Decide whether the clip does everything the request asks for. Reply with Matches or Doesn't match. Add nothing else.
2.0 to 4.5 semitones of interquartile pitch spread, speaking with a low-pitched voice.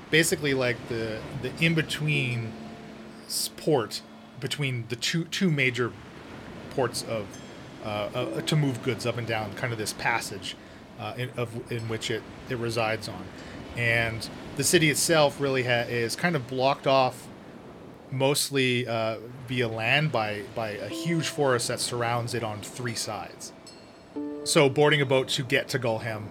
Matches